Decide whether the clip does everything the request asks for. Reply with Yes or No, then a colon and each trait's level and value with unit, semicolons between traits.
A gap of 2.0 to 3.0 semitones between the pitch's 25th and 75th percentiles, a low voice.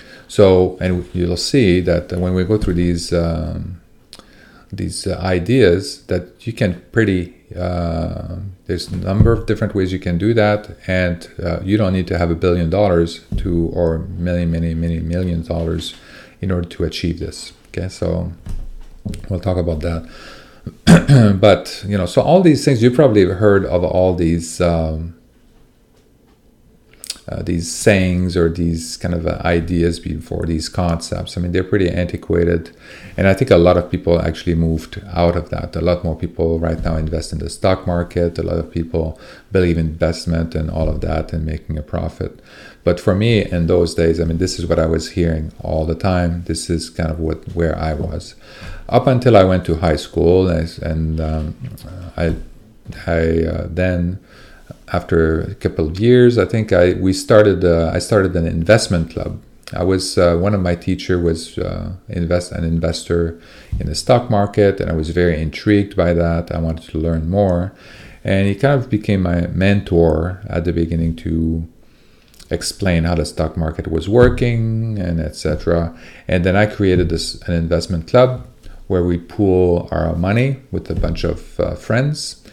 Yes: narrow, 2.5 semitones; very low, 90 Hz